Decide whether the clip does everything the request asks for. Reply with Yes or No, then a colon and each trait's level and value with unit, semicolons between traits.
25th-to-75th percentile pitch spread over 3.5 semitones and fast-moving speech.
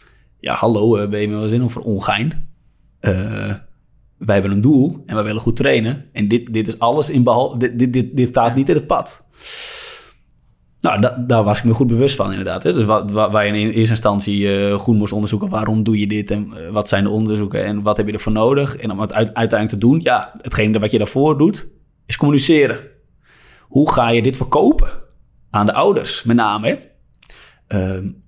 No: average, 3.2 semitones; fast, 210 wpm